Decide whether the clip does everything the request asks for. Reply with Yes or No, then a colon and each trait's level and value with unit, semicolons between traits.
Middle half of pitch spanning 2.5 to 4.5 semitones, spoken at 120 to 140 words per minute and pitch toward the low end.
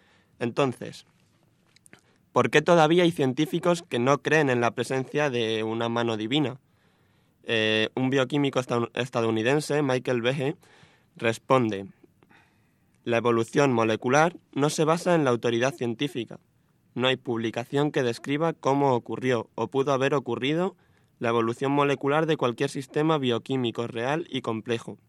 Yes: average, 3.8 semitones; average, 130 wpm; low, 130 Hz